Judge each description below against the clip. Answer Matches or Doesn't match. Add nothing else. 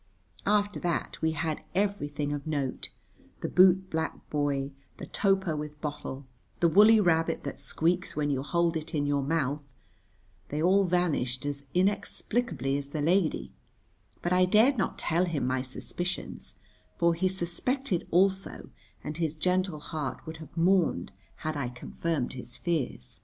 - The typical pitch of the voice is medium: Matches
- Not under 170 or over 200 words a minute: Doesn't match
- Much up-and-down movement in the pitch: Doesn't match